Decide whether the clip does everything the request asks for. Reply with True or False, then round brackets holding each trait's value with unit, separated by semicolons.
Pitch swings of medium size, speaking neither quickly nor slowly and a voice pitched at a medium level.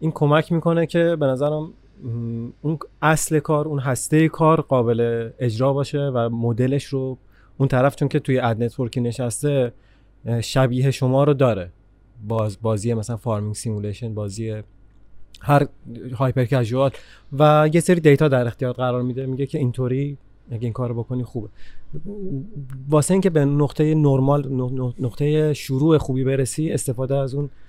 False (3.8 semitones; 145 wpm; 130 Hz)